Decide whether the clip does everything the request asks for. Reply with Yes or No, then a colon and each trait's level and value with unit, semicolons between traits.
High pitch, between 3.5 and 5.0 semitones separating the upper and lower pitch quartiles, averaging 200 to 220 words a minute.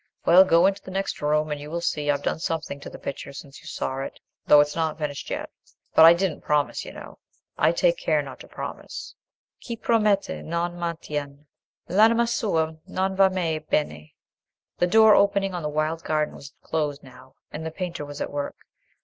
No: medium, 160 Hz; average, 4.3 semitones; fast, 205 wpm